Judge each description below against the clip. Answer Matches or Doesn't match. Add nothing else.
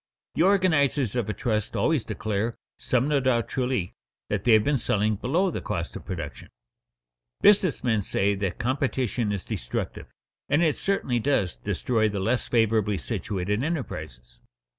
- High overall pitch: Doesn't match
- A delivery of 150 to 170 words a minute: Matches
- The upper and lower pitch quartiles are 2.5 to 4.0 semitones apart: Doesn't match